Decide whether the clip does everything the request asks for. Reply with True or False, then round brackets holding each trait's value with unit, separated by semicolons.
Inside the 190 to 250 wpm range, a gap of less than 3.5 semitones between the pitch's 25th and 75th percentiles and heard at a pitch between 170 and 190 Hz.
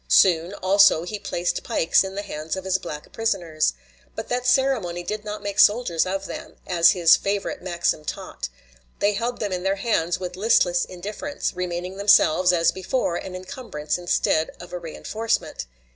False (170 wpm; 2.9 semitones; 185 Hz)